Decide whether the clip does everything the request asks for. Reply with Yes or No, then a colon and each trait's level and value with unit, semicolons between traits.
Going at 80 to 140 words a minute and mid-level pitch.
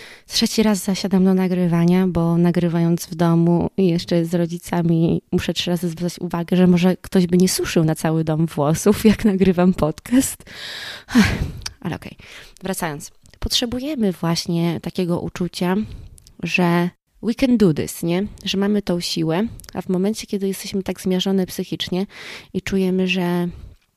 No: average, 150 wpm; medium, 180 Hz